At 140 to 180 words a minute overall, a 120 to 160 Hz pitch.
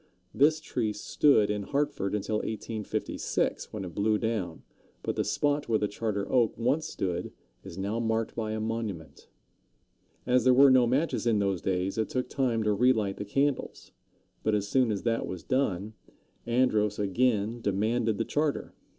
No: average, 170 wpm; low, 110 Hz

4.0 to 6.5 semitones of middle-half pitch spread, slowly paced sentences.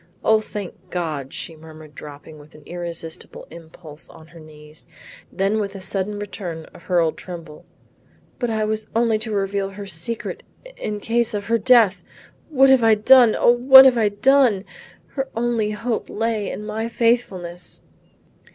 No: average, 5.1 semitones; average, 165 wpm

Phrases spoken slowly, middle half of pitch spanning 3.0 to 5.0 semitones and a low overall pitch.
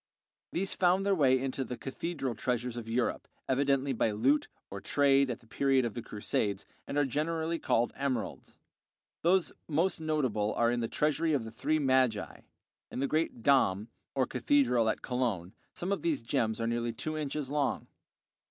No: average, 175 wpm; average, 4.3 semitones; low, 130 Hz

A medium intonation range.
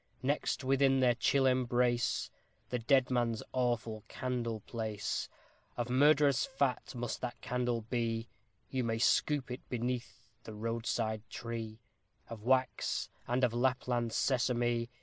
No: narrow, 1.9 semitones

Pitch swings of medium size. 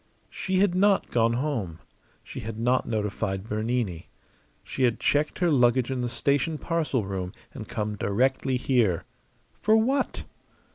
No: wide, 5.8 semitones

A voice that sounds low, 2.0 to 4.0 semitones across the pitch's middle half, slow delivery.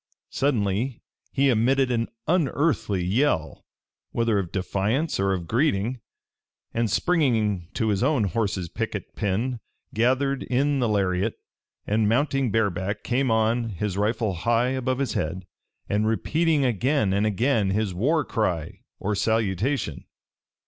No: low, 115 Hz; average, 4.8 semitones; slow, 130 wpm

